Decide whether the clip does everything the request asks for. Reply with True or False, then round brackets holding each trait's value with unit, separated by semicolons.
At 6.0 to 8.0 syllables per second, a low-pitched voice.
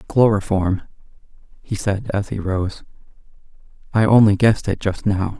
False (4.7 syllables/s; 100 Hz)